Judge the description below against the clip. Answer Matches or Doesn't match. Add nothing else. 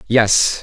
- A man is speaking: Matches